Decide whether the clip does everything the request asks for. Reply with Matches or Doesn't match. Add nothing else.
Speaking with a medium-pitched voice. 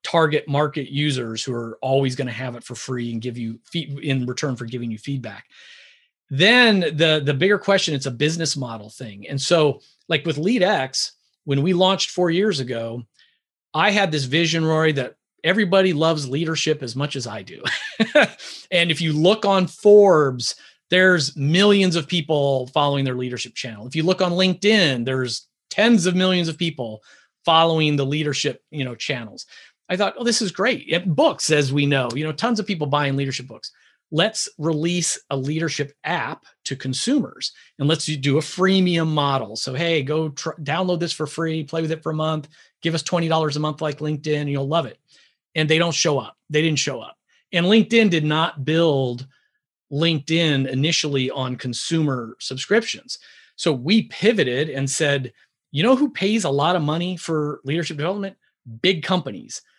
Matches